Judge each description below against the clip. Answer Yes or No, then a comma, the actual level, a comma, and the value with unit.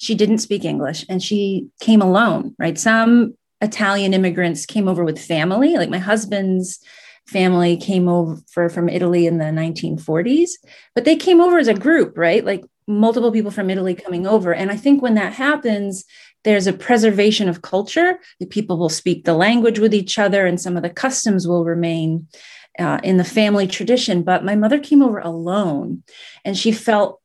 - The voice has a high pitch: Yes, high, 200 Hz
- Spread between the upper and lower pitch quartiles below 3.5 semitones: No, average, 4.0 semitones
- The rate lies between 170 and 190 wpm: Yes, average, 185 wpm